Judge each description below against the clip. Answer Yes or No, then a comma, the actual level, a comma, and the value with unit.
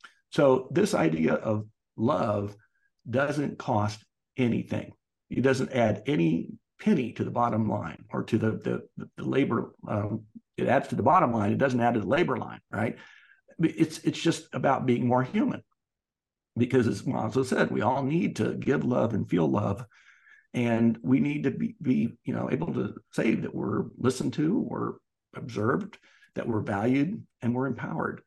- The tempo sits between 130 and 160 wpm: No, average, 170 wpm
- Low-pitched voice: Yes, low, 120 Hz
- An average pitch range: Yes, average, 3.8 semitones